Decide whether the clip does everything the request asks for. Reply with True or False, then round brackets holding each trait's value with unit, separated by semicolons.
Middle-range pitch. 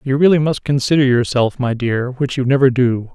False (130 Hz)